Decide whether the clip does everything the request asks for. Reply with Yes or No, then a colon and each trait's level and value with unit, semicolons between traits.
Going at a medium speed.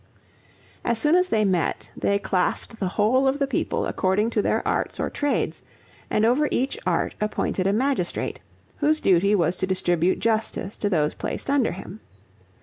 Yes: average, 170 wpm